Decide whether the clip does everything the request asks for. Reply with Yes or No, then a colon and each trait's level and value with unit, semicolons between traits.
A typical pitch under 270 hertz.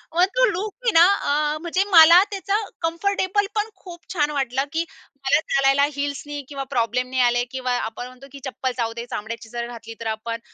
No: very high, 275 Hz